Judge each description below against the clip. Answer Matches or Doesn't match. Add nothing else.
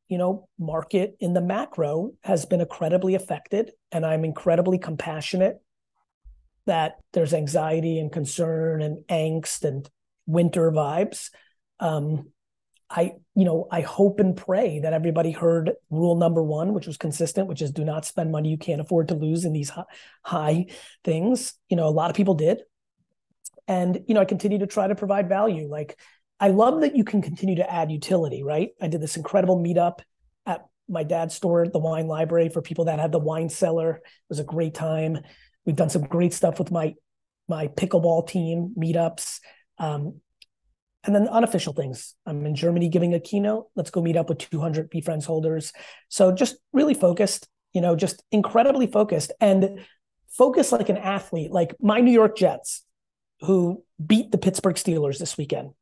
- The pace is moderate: Matches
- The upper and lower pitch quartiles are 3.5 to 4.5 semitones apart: Doesn't match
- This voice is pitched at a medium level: Matches